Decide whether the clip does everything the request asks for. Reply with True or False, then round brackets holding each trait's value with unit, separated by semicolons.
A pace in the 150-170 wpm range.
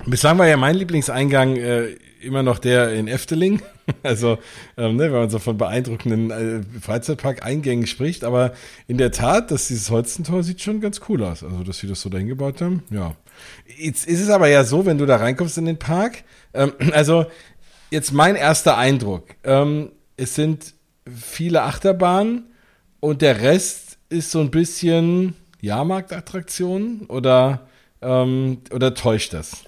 True (160 wpm)